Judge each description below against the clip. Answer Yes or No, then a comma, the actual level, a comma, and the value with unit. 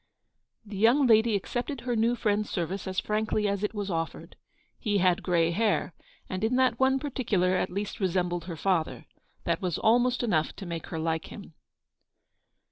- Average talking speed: Yes, average, 175 wpm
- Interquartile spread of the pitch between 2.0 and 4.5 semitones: Yes, average, 4.2 semitones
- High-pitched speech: Yes, high, 205 Hz